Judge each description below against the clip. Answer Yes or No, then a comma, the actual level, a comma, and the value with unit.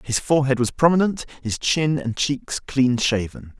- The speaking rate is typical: Yes, average, 165 wpm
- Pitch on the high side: No, low, 135 Hz